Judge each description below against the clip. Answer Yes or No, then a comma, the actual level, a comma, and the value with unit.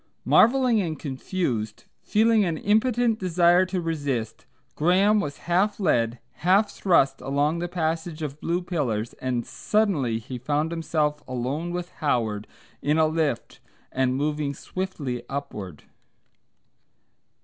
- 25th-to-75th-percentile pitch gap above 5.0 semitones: Yes, wide, 5.5 semitones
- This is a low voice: No, medium, 155 Hz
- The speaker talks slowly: Yes, slow, 125 wpm